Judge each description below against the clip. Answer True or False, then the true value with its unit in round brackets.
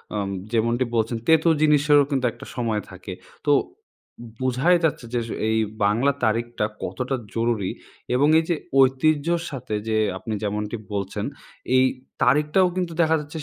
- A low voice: True (125 Hz)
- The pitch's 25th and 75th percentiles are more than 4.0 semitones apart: True (5.1 semitones)